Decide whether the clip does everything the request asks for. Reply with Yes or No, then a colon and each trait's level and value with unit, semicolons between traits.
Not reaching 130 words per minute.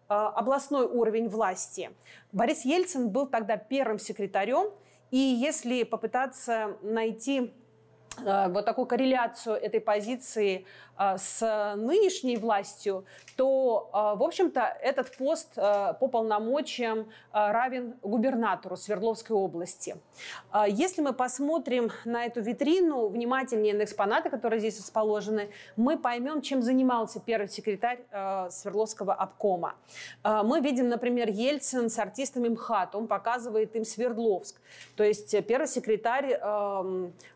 Yes: slow, 110 wpm